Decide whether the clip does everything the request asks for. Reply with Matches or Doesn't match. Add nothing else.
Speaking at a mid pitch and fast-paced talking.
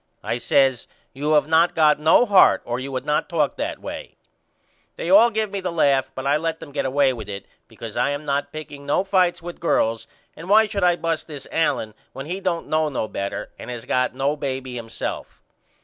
Matches